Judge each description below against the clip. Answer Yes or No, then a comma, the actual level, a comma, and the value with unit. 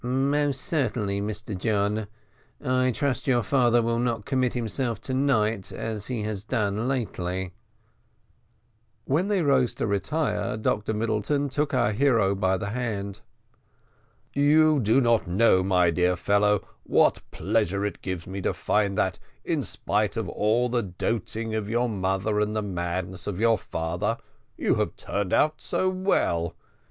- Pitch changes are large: No, average, 4.3 semitones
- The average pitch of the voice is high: No, low, 110 Hz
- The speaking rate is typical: Yes, average, 150 wpm